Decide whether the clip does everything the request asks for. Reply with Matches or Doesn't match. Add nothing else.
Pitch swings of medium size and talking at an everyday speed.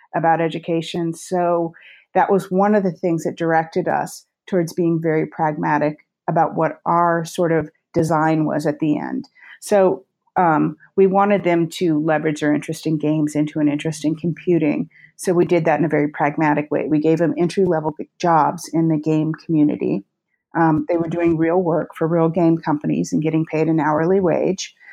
Doesn't match